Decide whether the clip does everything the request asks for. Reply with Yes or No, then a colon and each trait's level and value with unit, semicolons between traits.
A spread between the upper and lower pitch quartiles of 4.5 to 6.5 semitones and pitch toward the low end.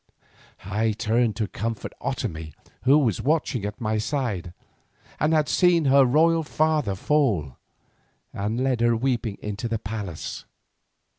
Yes: average, 5.2 semitones; low, 115 Hz